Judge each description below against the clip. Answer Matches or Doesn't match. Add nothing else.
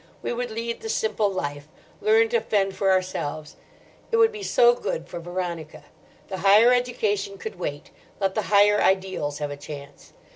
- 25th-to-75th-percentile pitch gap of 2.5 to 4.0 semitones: Doesn't match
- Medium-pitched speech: Doesn't match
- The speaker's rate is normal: Matches